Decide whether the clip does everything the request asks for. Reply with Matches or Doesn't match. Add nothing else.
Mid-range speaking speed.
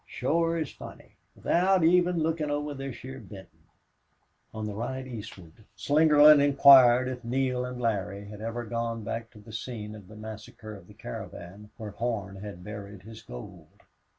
Matches